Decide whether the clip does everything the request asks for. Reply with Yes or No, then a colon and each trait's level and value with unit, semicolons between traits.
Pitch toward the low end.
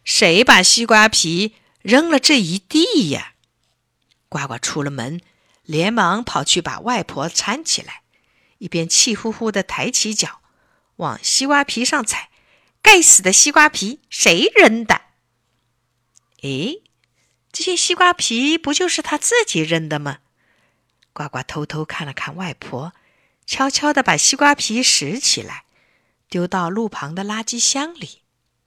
No: high, 225 Hz